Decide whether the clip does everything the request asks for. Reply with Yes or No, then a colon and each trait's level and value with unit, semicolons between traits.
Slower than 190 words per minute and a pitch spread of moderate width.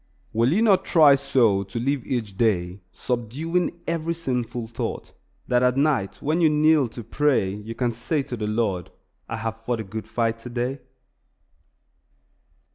Yes: average, 160 wpm; average, 4.6 semitones